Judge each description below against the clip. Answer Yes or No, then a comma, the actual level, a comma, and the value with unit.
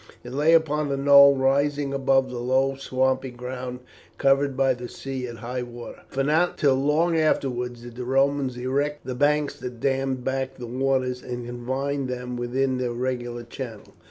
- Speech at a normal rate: Yes, average, 175 wpm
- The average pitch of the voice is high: No, low, 130 Hz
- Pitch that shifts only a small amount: Yes, narrow, 1.9 semitones